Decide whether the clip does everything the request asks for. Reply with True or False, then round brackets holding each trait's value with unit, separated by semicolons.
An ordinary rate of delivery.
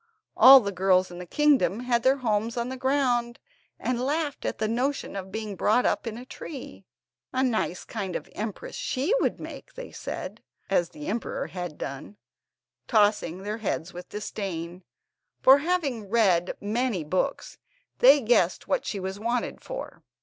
True (165 wpm)